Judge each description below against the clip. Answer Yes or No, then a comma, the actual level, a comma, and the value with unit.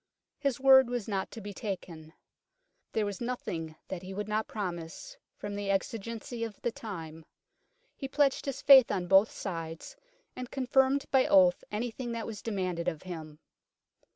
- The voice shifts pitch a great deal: Yes, wide, 5.8 semitones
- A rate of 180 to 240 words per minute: No, average, 165 wpm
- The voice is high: Yes, high, 215 Hz